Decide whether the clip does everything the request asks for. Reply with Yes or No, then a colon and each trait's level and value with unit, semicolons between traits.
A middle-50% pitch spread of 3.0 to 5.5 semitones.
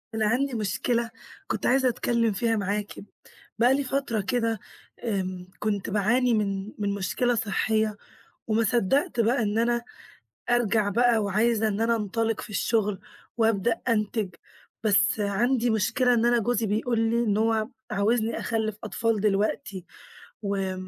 No: narrow, 2.5 semitones